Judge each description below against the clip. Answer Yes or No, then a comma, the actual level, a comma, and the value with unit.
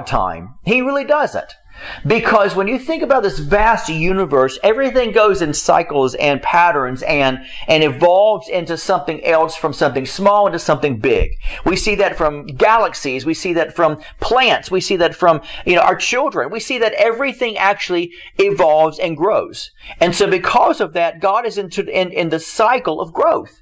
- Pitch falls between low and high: Yes, medium, 180 Hz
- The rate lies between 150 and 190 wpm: Yes, average, 180 wpm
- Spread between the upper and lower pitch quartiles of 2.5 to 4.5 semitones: No, average, 5.2 semitones